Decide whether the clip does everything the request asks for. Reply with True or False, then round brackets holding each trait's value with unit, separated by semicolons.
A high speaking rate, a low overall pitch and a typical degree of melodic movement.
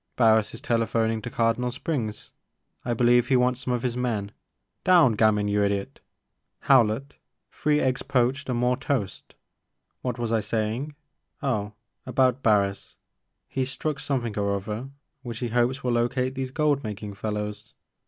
False (165 wpm; 120 Hz; 3.2 semitones)